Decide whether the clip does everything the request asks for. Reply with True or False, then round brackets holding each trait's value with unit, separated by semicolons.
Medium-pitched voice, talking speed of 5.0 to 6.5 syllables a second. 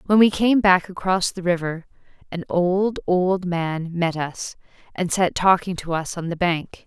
False (180 Hz; 4.2 syllables/s)